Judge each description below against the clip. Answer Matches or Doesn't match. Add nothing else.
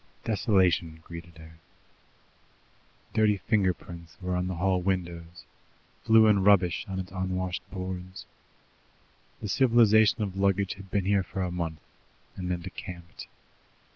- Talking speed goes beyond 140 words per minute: Doesn't match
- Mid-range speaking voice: Doesn't match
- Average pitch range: Doesn't match